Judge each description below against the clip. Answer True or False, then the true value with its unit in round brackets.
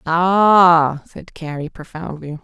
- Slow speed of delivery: True (100 wpm)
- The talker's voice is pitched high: False (165 Hz)